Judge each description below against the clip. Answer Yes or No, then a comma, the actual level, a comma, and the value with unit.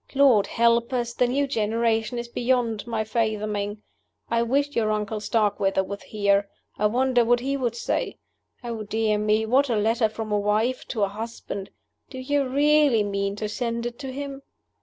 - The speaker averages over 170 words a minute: Yes, average, 180 wpm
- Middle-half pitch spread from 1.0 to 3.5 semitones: Yes, average, 2.8 semitones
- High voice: Yes, high, 230 Hz